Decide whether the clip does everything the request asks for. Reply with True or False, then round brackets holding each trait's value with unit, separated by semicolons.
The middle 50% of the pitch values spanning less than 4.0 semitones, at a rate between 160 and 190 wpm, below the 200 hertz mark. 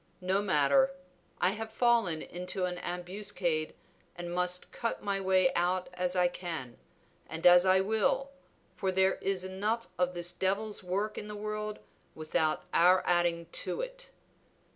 False (2.8 semitones; 150 wpm; 185 Hz)